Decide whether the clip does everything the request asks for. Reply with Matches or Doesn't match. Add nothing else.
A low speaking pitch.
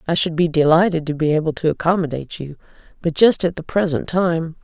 Doesn't match